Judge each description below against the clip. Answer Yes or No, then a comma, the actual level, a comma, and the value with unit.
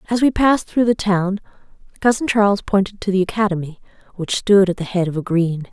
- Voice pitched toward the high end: Yes, high, 200 Hz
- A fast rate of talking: Yes, fast, 210 wpm